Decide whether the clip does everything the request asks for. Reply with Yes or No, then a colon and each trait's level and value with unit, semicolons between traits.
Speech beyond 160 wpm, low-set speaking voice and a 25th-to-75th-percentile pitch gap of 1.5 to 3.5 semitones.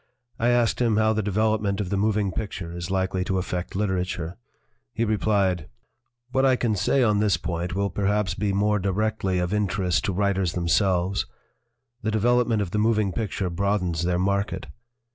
Yes: average, 170 wpm; low, 100 Hz; average, 2.8 semitones